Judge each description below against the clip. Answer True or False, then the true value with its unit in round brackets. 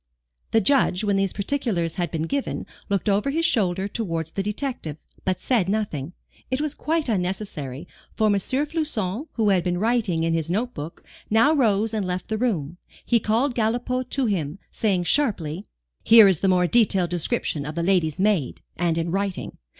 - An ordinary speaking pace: True (180 wpm)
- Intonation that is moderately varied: True (4.9 semitones)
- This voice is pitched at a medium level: False (200 Hz)